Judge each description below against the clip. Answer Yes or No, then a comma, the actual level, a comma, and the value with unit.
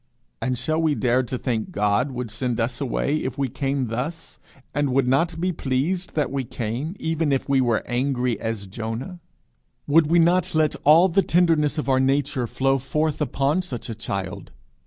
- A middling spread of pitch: Yes, average, 4.2 semitones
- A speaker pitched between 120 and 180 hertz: Yes, low, 135 Hz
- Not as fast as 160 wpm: No, average, 185 wpm